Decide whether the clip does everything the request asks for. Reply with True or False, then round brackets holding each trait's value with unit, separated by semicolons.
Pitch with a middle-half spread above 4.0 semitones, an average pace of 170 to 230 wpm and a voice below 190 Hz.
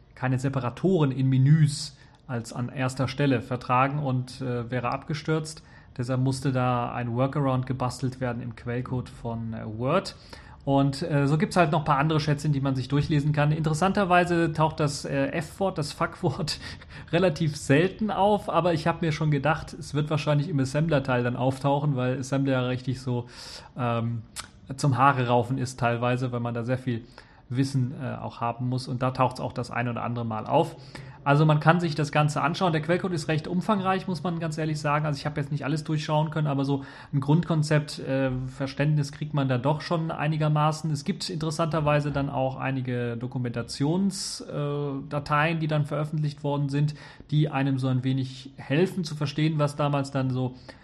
False (3.2 semitones; 185 wpm; 140 Hz)